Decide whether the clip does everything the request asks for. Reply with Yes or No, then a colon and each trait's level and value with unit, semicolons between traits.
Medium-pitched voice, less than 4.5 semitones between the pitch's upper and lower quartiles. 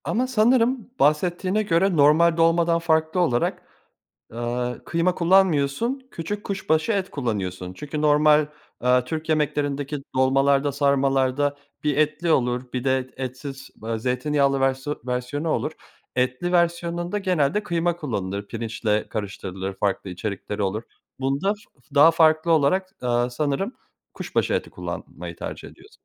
No: medium, 145 Hz; average, 5.1 semitones